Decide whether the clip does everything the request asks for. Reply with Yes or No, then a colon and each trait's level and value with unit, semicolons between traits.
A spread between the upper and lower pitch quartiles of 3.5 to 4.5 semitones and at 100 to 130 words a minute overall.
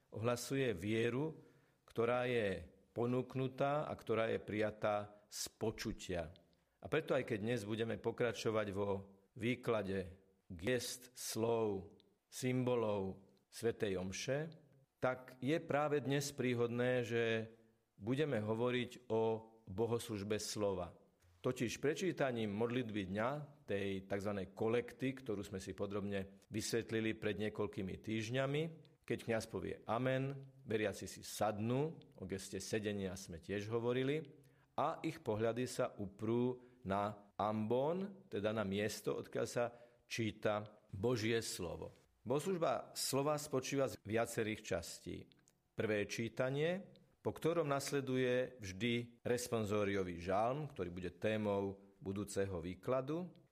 Yes: average, 3.9 semitones; slow, 110 wpm